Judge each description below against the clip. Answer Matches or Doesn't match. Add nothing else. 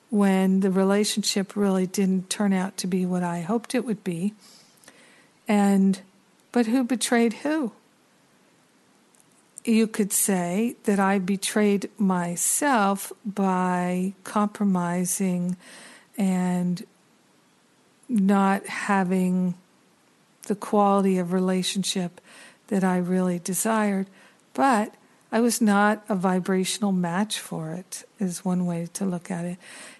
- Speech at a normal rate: Doesn't match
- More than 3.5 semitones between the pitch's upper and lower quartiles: Doesn't match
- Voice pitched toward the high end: Matches